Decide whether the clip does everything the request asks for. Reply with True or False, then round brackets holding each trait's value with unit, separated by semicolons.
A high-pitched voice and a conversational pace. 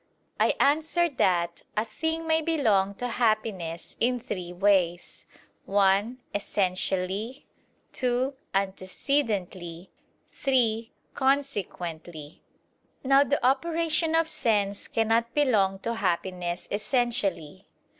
False (215 Hz; 95 wpm)